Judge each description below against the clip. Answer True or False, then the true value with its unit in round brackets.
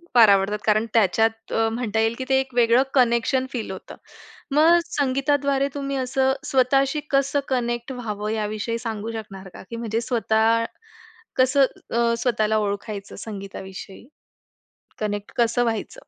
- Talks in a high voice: True (230 Hz)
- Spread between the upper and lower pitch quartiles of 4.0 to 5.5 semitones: False (3.3 semitones)